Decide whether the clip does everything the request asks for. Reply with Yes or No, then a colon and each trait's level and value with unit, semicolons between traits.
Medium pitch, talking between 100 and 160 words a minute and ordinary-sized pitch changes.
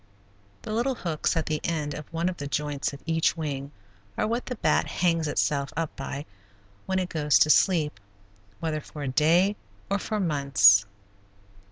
No: medium, 155 Hz; average, 175 wpm; average, 3.7 semitones